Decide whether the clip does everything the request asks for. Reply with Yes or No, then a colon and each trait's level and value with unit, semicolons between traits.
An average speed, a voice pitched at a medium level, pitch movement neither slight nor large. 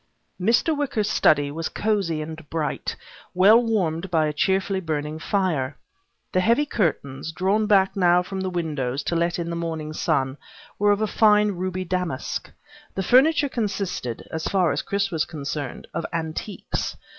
Yes: average, 160 wpm; medium, 180 Hz; average, 4.4 semitones